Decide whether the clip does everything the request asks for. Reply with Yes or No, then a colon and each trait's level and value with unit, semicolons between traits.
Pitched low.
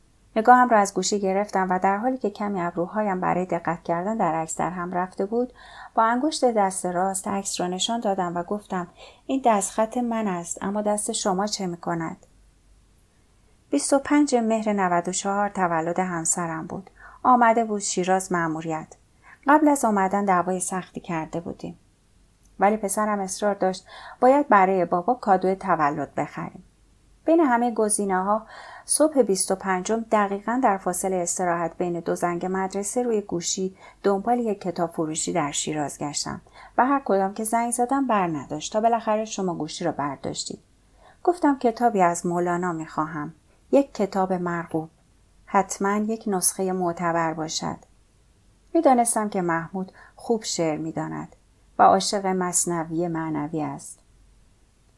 No: high, 190 Hz